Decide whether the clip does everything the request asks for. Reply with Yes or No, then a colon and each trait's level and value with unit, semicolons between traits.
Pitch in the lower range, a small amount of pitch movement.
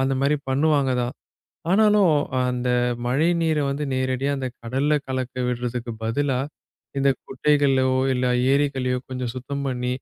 Yes: low, 130 Hz; narrow, 2.2 semitones